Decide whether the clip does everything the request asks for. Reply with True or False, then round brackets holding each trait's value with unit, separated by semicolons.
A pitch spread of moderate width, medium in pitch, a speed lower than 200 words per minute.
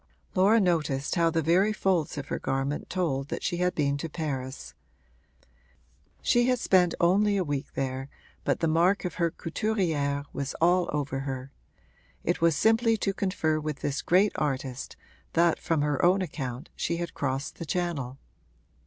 True (4.5 semitones; 165 Hz; 165 wpm)